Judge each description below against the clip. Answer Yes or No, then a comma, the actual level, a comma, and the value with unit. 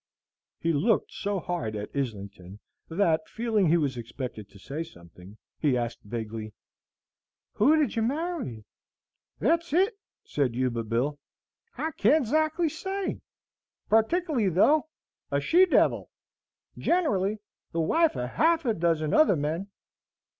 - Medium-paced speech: No, slow, 130 wpm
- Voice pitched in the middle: Yes, medium, 170 Hz